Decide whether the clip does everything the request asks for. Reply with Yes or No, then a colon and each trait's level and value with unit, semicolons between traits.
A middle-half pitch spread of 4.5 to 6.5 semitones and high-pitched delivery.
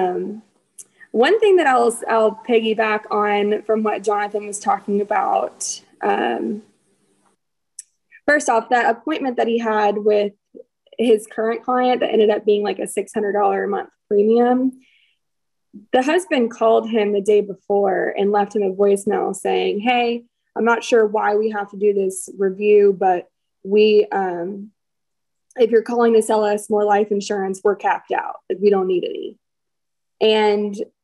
No: narrow, 2.4 semitones; high, 215 Hz